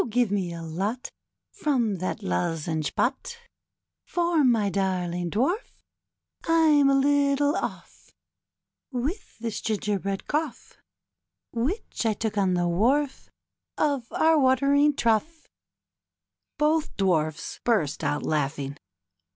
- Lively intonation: Yes, wide, 8.1 semitones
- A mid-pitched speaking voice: No, high, 230 Hz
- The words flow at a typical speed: No, slow, 110 wpm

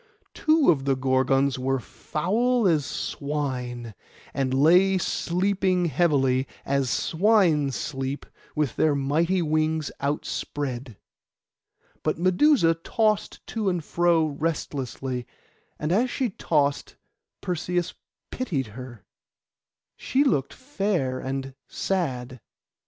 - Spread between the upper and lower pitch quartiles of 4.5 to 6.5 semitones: Yes, average, 5.3 semitones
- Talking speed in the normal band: No, slow, 105 wpm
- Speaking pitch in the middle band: Yes, medium, 150 Hz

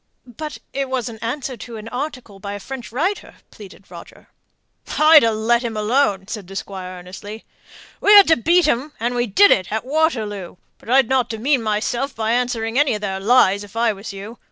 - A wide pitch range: No, average, 4.4 semitones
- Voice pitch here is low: No, high, 230 Hz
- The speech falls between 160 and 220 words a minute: Yes, fast, 205 wpm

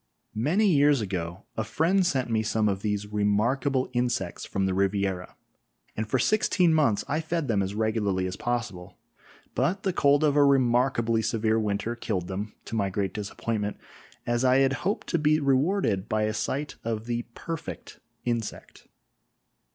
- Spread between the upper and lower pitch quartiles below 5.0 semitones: No, average, 5.3 semitones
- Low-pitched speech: Yes, low, 115 Hz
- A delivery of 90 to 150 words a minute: No, average, 165 wpm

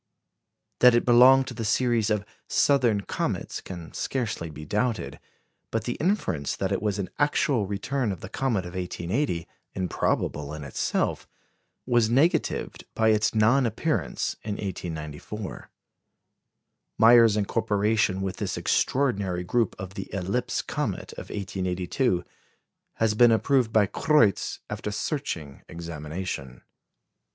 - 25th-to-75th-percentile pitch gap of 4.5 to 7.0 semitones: Yes, average, 5.0 semitones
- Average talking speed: No, slow, 125 wpm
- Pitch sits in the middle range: No, low, 105 Hz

